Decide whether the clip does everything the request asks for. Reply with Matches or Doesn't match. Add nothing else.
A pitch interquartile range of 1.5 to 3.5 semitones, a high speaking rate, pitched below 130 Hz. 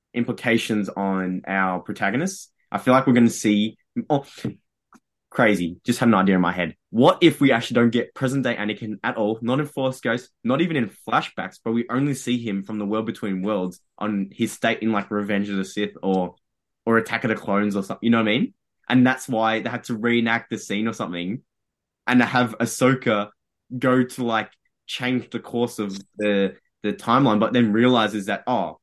Matches